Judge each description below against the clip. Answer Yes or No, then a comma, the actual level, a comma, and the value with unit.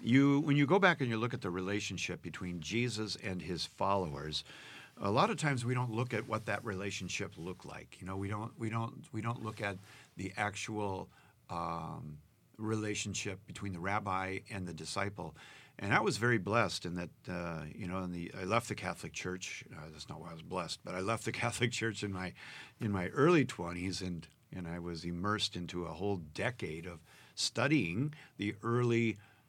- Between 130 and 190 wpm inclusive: No, average, 200 wpm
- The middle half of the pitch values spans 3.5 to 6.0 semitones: Yes, average, 4.1 semitones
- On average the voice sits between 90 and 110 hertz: Yes, low, 100 Hz